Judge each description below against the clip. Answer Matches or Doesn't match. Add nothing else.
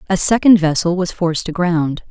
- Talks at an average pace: Matches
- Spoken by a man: Doesn't match